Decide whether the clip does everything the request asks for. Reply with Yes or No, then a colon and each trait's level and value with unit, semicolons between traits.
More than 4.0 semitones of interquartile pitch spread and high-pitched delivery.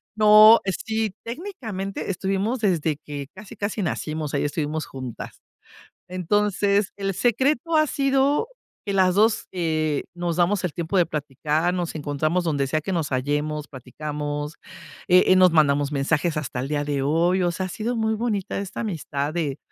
No: wide, 5.5 semitones; medium, 175 Hz